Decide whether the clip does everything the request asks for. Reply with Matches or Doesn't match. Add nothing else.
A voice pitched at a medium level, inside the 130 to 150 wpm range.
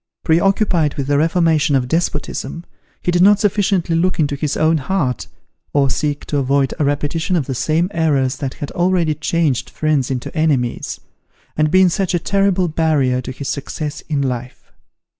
Doesn't match